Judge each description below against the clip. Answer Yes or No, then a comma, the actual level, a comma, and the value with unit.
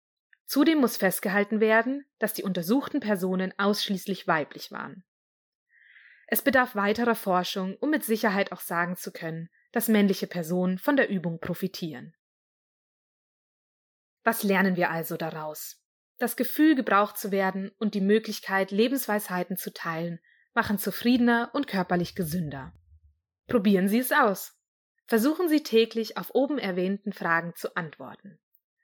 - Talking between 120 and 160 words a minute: Yes, average, 130 wpm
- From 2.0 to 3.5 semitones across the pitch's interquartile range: No, average, 4.4 semitones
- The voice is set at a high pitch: Yes, high, 200 Hz